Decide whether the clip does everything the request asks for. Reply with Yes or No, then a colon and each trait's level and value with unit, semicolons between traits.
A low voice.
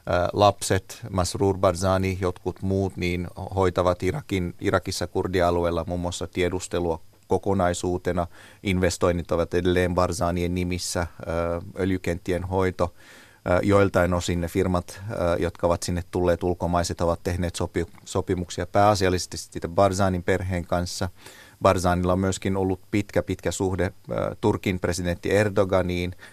Yes: very low, 90 Hz